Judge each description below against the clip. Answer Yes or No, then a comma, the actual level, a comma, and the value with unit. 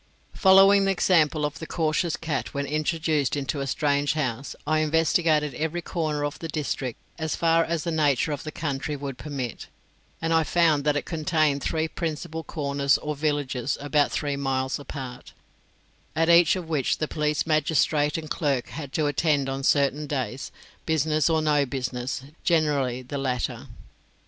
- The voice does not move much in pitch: Yes, narrow, 2.3 semitones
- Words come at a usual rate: Yes, average, 165 wpm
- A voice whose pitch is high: No, medium, 150 Hz